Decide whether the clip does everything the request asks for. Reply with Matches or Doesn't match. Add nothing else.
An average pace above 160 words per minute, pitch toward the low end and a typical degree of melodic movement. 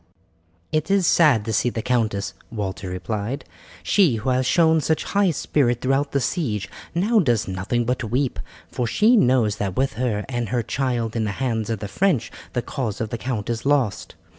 Matches